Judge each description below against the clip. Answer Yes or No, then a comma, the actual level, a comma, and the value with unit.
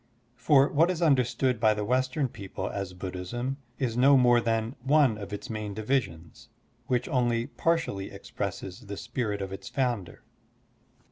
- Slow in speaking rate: No, average, 150 wpm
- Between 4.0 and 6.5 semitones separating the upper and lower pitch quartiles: Yes, average, 4.6 semitones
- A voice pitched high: No, low, 120 Hz